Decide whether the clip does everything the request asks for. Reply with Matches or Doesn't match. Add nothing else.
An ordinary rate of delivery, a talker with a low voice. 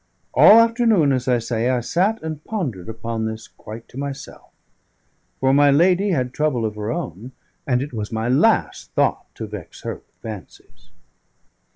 Matches